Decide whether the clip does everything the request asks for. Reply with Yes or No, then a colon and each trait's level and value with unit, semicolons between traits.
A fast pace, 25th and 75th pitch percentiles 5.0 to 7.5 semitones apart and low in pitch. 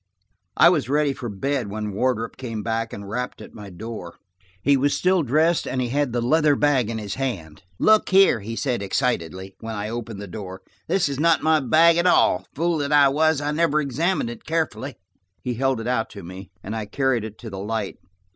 Yes: fast, 220 wpm; wide, 5.4 semitones; low, 125 Hz